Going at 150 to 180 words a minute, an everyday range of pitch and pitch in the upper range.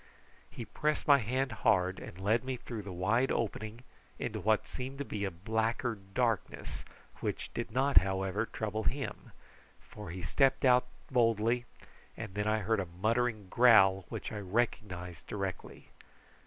No: average, 155 wpm; average, 4.0 semitones; low, 110 Hz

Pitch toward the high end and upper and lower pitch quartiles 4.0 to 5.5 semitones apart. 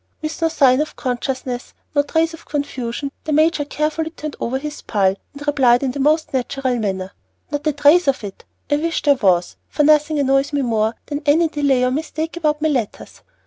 No: very high, 285 Hz; average, 3.3 semitones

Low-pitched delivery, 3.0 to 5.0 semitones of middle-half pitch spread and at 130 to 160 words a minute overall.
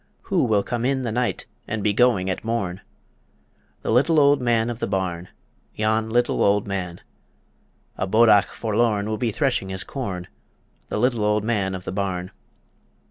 No: low, 110 Hz; average, 3.6 semitones; average, 170 wpm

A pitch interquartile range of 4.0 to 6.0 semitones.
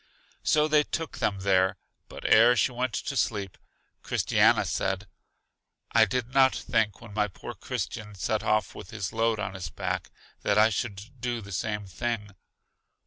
No: average, 3.2 semitones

